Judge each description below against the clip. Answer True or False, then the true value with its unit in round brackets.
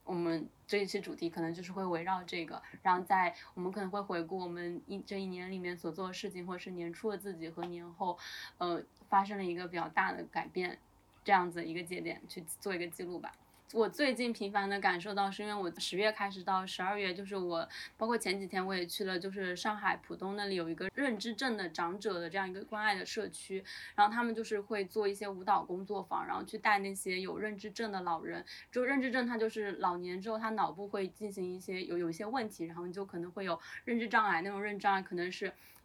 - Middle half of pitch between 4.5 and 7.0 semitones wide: False (2.6 semitones)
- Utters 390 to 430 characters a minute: False (350 characters per minute)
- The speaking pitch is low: False (190 Hz)